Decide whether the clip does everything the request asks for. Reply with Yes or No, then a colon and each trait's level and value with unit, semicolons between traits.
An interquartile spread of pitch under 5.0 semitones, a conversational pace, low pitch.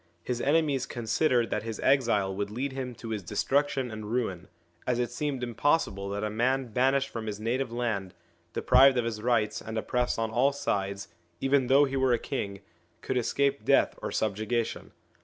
Yes: average, 3.8 semitones; average, 175 wpm; low, 120 Hz